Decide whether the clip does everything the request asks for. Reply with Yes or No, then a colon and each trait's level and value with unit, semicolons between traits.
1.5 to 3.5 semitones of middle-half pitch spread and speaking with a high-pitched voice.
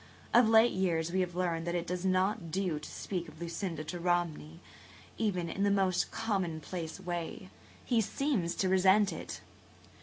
No: average, 2.7 semitones; medium, 180 Hz